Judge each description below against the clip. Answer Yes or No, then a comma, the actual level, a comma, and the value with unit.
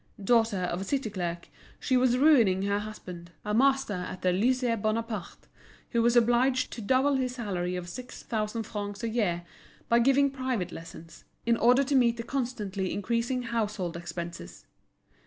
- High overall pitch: Yes, high, 225 Hz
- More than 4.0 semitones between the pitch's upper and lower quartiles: Yes, average, 5.0 semitones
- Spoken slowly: No, average, 165 wpm